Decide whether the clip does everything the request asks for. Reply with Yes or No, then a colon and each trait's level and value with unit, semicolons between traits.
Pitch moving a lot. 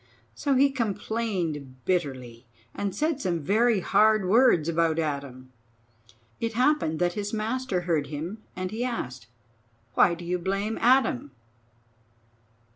Yes: wide, 6.5 semitones